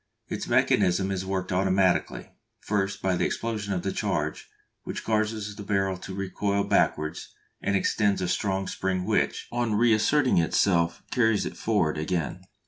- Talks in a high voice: No, very low, 95 Hz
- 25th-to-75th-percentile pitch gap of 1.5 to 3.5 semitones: Yes, narrow, 2.4 semitones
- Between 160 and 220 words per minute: No, average, 150 wpm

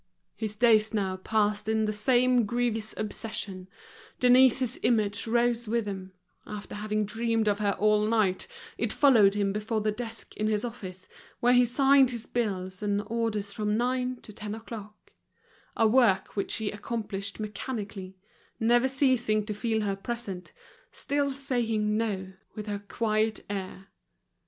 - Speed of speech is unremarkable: Yes, average, 150 wpm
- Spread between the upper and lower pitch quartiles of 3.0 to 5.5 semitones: No, narrow, 2.5 semitones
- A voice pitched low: No, high, 215 Hz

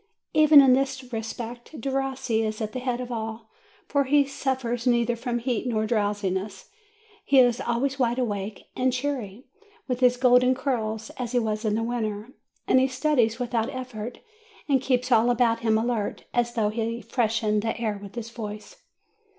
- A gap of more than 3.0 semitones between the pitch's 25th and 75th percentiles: No, average, 2.7 semitones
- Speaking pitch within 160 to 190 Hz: No, high, 240 Hz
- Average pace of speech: Yes, average, 175 wpm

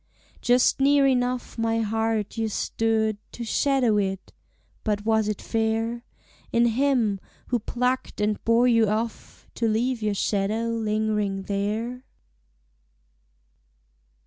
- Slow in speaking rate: Yes, slow, 120 wpm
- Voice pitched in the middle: No, high, 225 Hz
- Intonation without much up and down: Yes, narrow, 2.2 semitones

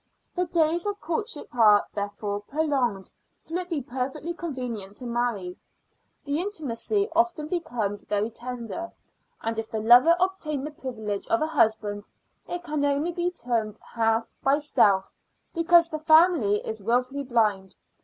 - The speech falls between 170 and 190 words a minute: No, average, 145 wpm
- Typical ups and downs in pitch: No, wide, 7.1 semitones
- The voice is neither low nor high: No, very high, 260 Hz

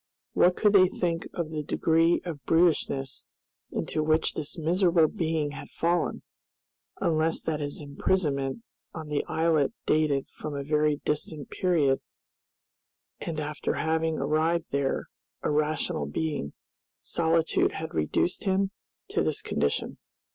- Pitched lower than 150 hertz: No, medium, 155 Hz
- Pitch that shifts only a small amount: Yes, narrow, 2.2 semitones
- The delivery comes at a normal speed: No, slow, 130 wpm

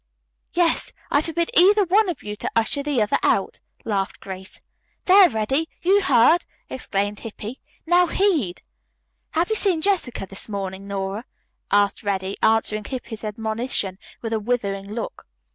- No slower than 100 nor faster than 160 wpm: Yes, average, 145 wpm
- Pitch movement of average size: No, wide, 8.6 semitones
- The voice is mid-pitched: No, high, 230 Hz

